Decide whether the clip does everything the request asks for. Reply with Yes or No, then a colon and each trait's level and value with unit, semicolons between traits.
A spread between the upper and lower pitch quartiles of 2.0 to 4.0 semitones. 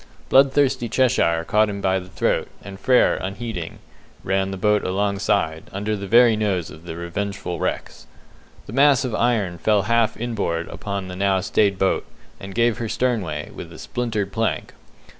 Yes: average, 3.7 semitones